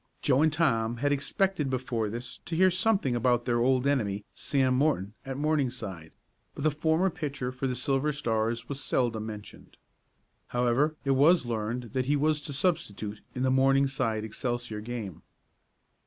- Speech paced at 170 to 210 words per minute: No, average, 160 wpm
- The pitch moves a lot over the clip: No, average, 3.9 semitones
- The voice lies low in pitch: Yes, low, 130 Hz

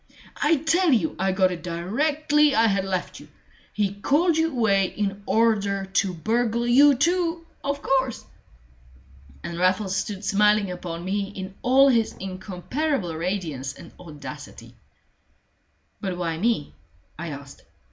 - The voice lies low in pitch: No, high, 205 Hz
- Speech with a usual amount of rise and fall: No, wide, 6.4 semitones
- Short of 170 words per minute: Yes, slow, 135 wpm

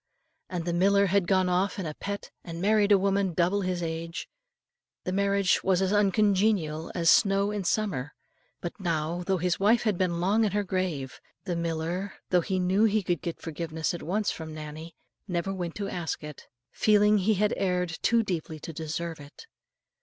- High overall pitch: No, medium, 180 Hz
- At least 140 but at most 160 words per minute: No, average, 190 wpm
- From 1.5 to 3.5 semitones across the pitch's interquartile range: Yes, average, 3.1 semitones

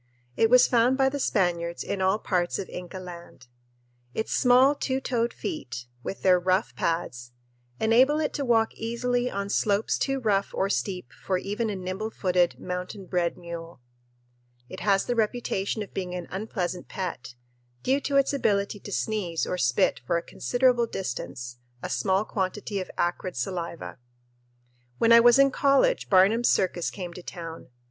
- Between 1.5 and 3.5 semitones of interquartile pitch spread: No, average, 4.8 semitones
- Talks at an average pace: Yes, average, 165 wpm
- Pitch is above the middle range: Yes, high, 195 Hz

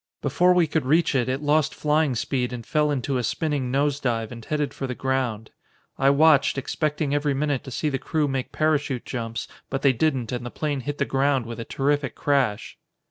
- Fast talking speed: Yes, fast, 210 wpm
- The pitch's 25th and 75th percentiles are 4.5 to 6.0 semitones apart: No, average, 2.9 semitones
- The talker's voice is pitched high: No, low, 135 Hz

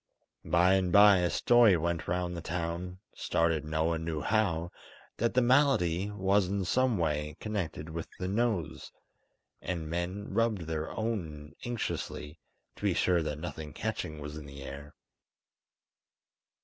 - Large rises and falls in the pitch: No, average, 4.4 semitones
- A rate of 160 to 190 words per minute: No, average, 150 wpm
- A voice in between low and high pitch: No, very low, 85 Hz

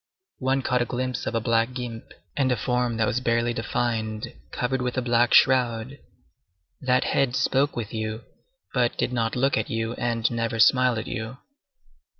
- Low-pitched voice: Yes, low, 120 Hz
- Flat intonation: Yes, narrow, 1.9 semitones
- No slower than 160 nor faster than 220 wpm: Yes, average, 175 wpm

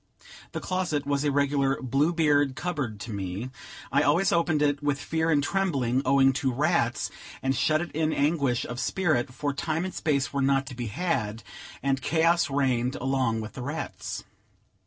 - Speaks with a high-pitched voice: No, medium, 140 Hz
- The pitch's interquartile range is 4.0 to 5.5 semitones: No, average, 3.5 semitones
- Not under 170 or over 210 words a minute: Yes, average, 180 wpm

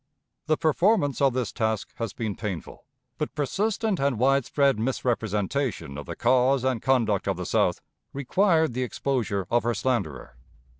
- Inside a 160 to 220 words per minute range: No, average, 150 wpm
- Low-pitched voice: Yes, low, 130 Hz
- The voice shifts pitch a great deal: No, average, 4.1 semitones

